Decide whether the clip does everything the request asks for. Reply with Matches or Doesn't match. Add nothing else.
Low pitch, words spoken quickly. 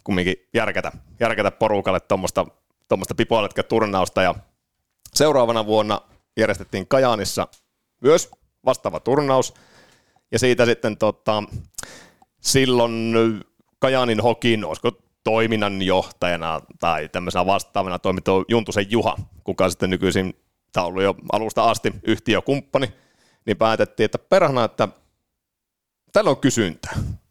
Doesn't match